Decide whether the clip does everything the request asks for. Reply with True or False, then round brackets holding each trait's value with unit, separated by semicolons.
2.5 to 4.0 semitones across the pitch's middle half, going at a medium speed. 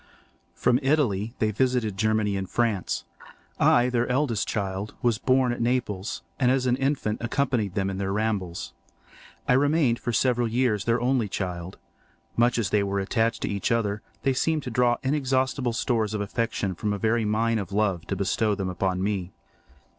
True (3.7 semitones; 175 wpm)